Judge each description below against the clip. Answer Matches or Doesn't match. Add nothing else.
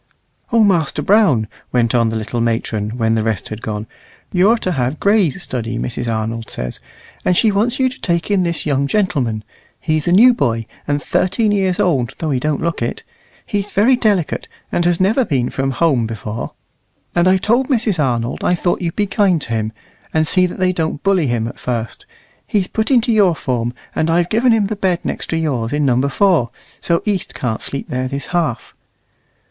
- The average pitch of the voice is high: Doesn't match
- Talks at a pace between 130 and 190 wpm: Doesn't match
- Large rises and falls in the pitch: Matches